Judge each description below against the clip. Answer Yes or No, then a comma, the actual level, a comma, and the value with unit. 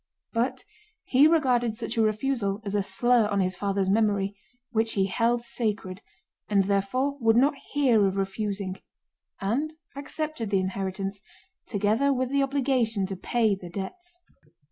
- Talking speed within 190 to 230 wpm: No, average, 145 wpm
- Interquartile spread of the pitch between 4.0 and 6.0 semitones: Yes, average, 4.5 semitones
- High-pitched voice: Yes, high, 220 Hz